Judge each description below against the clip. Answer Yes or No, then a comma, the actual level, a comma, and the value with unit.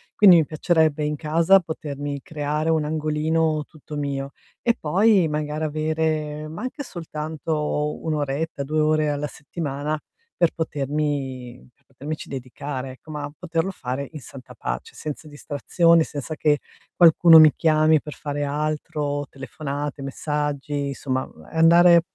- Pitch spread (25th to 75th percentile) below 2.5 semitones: Yes, narrow, 1.8 semitones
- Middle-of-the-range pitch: Yes, medium, 150 Hz